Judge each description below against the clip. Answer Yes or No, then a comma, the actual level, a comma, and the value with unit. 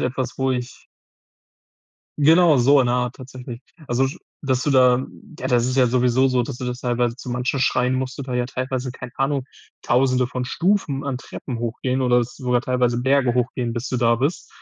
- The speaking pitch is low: Yes, low, 125 Hz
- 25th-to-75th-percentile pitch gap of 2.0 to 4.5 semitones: No, narrow, 1.4 semitones